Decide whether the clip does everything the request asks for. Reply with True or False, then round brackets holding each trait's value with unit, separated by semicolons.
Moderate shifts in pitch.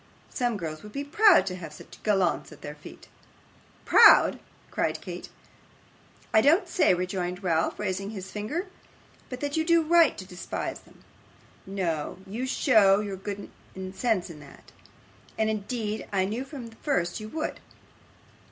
False (5.8 semitones)